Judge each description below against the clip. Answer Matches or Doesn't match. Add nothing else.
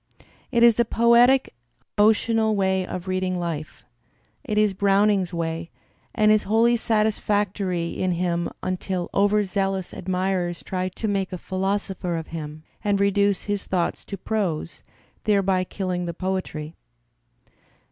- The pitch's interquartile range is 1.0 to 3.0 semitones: Matches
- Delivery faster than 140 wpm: Doesn't match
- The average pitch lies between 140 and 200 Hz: Matches